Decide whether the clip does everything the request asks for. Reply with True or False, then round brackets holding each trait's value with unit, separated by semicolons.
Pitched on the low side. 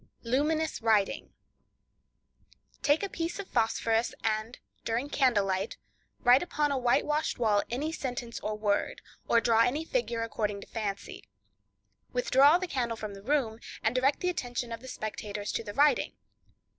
False (240 Hz)